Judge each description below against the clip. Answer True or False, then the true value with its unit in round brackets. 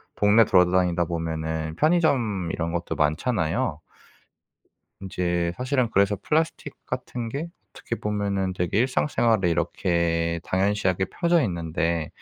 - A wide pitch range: False (5.0 semitones)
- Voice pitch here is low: True (95 Hz)